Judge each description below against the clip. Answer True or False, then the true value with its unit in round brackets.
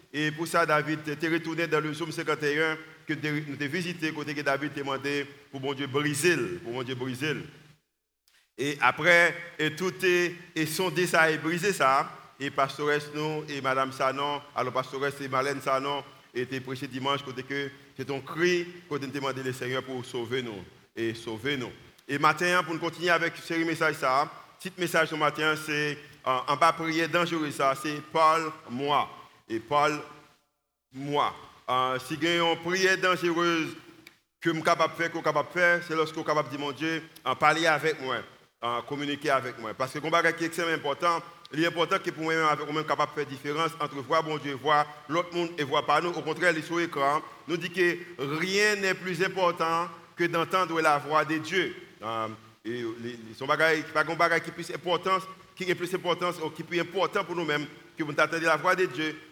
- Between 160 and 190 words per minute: True (185 wpm)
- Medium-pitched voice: True (155 Hz)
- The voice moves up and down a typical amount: True (3.1 semitones)